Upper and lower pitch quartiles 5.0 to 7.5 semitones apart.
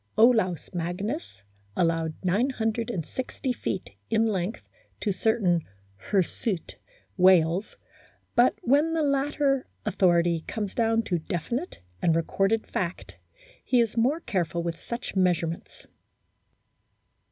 Yes: wide, 5.5 semitones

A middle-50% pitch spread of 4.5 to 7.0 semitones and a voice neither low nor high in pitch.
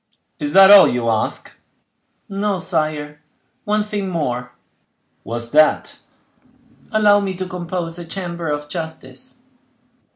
Yes: average, 4.9 semitones; medium, 175 Hz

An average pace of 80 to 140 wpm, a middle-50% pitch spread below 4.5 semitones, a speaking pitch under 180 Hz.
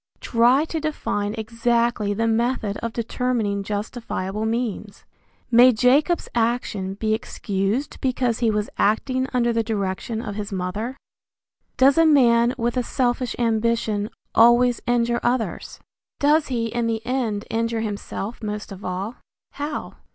No: slow, 135 wpm; average, 2.7 semitones; high, 230 Hz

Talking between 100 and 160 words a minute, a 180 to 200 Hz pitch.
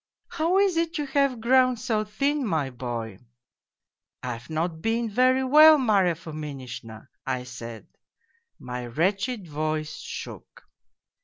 Yes: average, 150 wpm; high, 190 Hz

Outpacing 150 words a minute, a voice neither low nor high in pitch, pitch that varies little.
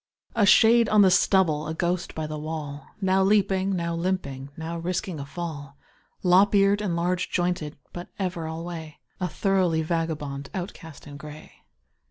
No: average, 160 wpm; medium, 170 Hz; average, 3.4 semitones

